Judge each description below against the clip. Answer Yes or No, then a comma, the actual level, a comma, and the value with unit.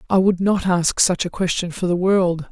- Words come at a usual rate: No, fast, 240 wpm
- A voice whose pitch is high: No, medium, 180 Hz